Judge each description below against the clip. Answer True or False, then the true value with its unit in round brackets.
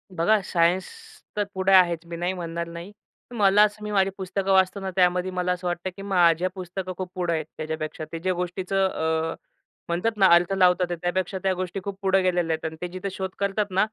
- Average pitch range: False (1.9 semitones)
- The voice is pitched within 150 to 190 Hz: True (185 Hz)